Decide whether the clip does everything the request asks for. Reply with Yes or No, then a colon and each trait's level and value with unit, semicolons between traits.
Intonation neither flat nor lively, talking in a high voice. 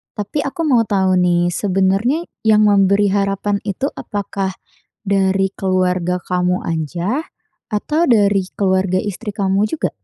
No: narrow, 1.9 semitones; high, 195 Hz